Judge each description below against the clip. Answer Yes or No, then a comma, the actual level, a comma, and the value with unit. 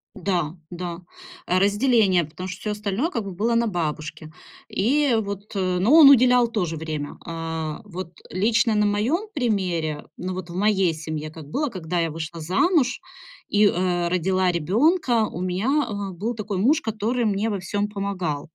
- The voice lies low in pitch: No, high, 190 Hz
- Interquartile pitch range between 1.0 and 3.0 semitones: No, average, 4.7 semitones